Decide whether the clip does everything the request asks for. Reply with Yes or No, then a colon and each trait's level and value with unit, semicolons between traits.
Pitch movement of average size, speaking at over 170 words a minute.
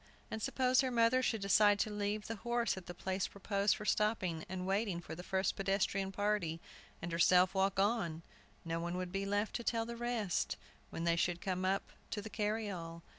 Yes: average, 3.0 semitones; average, 200 wpm